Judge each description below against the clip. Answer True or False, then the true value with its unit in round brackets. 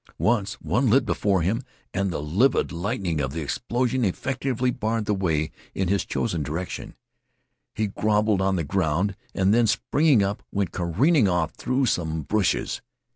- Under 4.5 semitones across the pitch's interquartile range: False (4.9 semitones)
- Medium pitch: False (100 Hz)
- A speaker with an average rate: True (160 wpm)